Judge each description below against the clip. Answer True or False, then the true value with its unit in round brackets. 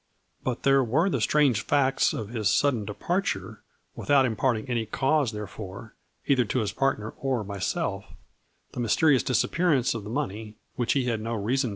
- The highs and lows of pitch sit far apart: False (4.0 semitones)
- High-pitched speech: False (120 Hz)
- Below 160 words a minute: False (190 wpm)